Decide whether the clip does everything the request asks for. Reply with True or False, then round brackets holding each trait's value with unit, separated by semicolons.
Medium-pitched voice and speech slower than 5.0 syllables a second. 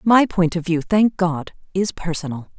True (175 Hz; 4.4 syllables/s)